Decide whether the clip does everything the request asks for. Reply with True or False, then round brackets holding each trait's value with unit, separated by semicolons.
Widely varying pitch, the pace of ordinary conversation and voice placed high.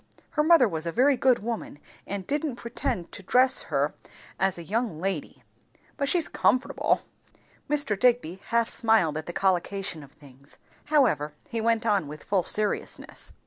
True (6.5 semitones; 160 wpm; 215 Hz)